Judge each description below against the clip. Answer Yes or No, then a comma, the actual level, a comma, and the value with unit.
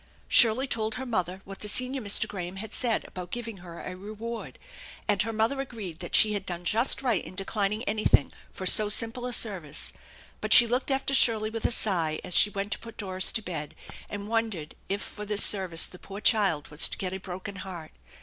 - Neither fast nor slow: No, fast, 215 wpm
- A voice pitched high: Yes, high, 205 Hz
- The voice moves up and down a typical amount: Yes, average, 3.6 semitones